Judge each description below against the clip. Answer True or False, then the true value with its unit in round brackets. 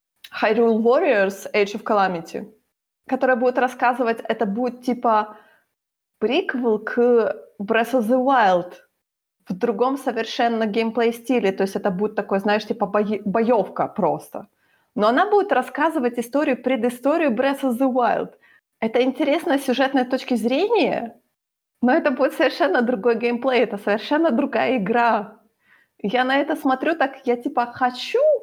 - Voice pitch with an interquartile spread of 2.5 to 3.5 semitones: True (2.9 semitones)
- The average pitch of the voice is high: True (245 Hz)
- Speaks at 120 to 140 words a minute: True (135 wpm)